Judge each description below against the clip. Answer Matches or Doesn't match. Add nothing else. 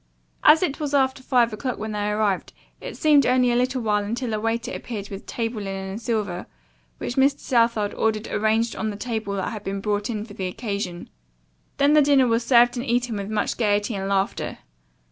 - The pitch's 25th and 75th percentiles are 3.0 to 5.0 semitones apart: Matches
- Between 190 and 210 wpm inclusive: Matches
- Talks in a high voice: Matches